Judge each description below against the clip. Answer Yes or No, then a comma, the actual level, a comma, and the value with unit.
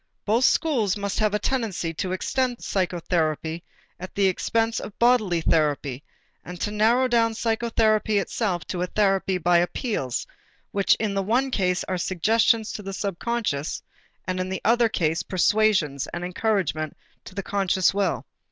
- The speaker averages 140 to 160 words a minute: Yes, average, 155 wpm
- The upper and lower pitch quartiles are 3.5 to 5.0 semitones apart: Yes, average, 4.0 semitones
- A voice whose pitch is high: Yes, high, 195 Hz